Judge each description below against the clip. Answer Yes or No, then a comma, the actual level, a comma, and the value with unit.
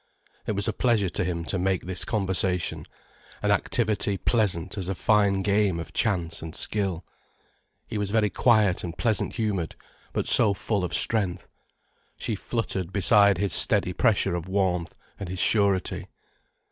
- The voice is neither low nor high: No, very low, 95 Hz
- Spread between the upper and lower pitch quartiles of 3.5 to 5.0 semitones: No, average, 2.7 semitones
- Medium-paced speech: Yes, average, 160 wpm